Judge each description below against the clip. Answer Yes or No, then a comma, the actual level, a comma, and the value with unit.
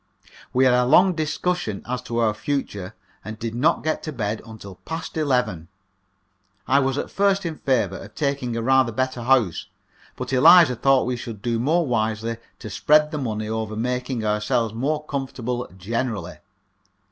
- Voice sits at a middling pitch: No, low, 125 Hz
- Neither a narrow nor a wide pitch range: Yes, average, 4.1 semitones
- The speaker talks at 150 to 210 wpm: Yes, average, 170 wpm